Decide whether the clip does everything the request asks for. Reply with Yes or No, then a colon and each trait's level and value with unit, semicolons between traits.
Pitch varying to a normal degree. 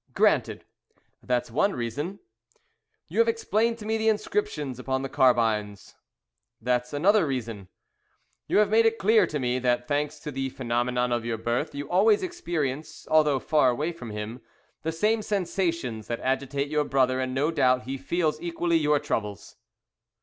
No: wide, 6.0 semitones